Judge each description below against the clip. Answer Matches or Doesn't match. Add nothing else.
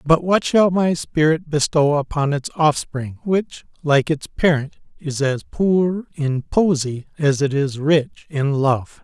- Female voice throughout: Doesn't match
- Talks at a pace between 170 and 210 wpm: Doesn't match